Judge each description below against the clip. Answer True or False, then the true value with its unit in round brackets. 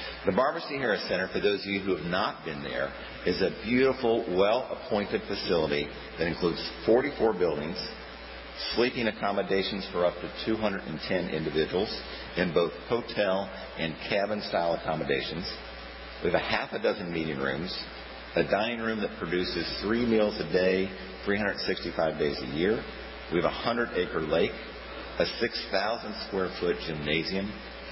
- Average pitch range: False (5.8 semitones)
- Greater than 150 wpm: False (140 wpm)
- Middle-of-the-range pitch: False (95 Hz)